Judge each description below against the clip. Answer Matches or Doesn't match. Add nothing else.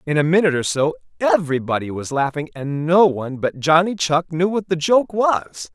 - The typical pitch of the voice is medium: Matches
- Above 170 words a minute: Matches